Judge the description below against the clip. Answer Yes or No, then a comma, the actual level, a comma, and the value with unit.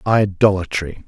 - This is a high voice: No, very low, 95 Hz